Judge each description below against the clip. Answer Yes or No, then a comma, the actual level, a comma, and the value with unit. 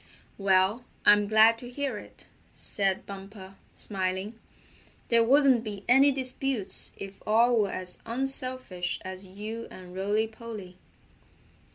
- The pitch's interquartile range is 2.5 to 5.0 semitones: Yes, average, 4.0 semitones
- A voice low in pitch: No, high, 215 Hz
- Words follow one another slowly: Yes, slow, 125 wpm